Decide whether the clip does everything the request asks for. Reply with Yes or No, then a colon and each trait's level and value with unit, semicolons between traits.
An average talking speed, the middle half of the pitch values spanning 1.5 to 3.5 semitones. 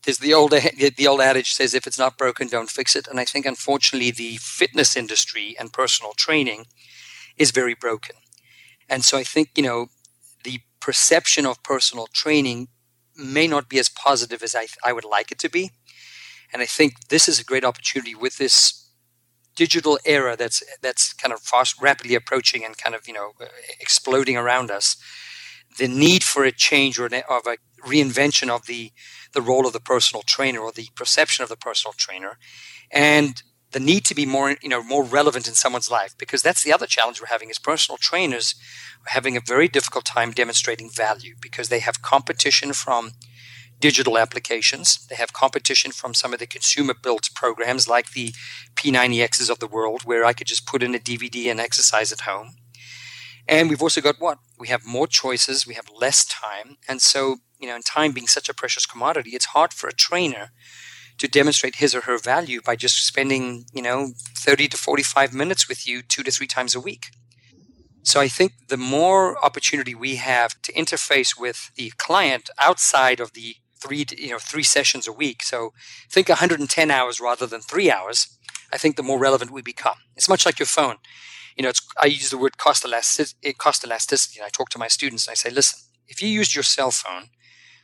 Yes: average, 195 wpm; average, 2.8 semitones